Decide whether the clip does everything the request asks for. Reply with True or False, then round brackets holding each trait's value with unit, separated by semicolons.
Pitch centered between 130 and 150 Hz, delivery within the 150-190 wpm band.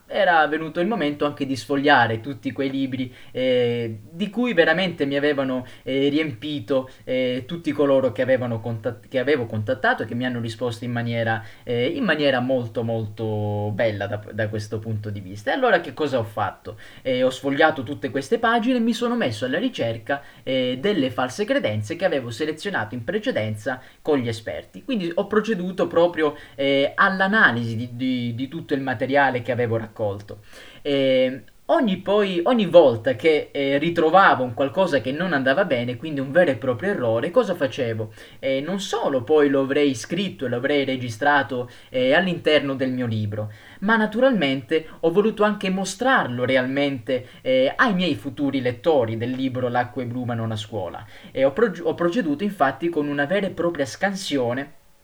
True (140 Hz; 170 wpm)